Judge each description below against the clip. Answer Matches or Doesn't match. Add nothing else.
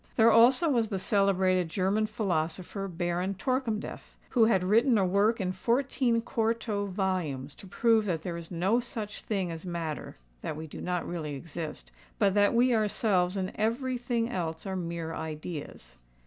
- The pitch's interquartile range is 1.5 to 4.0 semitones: Doesn't match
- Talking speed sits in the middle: Matches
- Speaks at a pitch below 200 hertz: Matches